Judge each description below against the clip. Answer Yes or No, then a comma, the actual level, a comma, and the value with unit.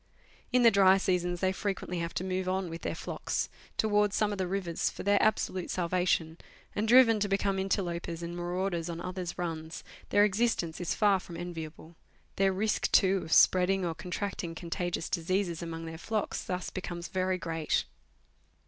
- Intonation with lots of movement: No, narrow, 2.4 semitones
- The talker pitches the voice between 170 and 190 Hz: Yes, medium, 185 Hz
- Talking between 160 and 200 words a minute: Yes, average, 175 wpm